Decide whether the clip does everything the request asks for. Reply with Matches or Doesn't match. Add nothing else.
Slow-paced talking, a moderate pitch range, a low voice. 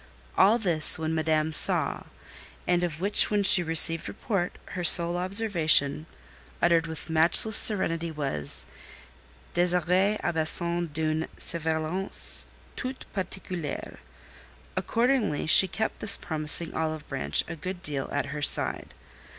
Doesn't match